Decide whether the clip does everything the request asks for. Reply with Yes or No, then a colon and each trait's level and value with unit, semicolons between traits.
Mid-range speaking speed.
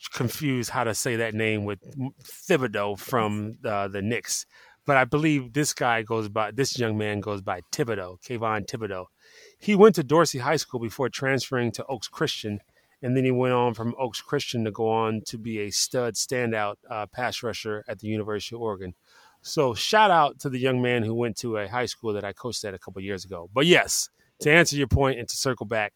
No: fast, 215 wpm